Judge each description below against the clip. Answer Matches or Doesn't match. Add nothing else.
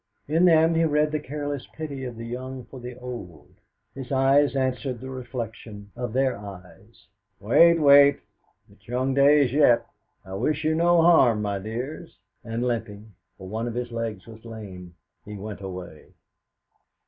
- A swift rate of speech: Doesn't match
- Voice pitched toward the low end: Matches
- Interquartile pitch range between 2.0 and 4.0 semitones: Doesn't match